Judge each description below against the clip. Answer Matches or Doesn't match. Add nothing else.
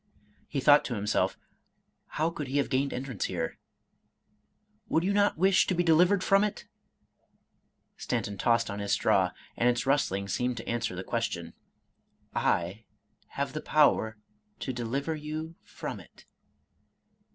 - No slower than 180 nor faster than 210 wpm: Doesn't match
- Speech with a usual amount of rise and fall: Doesn't match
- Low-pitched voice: Matches